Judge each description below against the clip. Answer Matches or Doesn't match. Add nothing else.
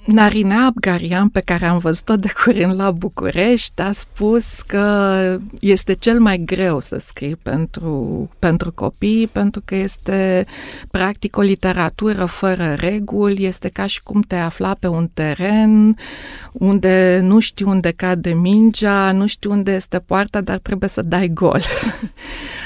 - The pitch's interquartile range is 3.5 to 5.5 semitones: Doesn't match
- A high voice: Matches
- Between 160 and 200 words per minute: Doesn't match